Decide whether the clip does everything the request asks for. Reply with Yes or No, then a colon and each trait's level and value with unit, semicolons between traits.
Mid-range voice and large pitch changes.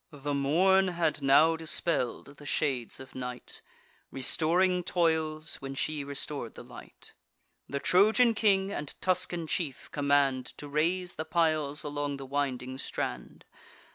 No: medium, 150 Hz; average, 3.7 semitones